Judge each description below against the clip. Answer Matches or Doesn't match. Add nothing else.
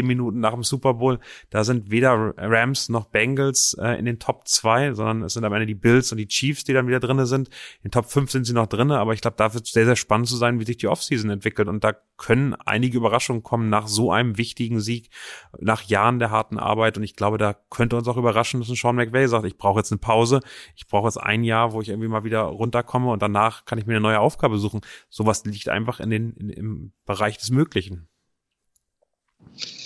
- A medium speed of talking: Doesn't match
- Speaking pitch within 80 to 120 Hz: Matches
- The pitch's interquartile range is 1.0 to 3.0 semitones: Matches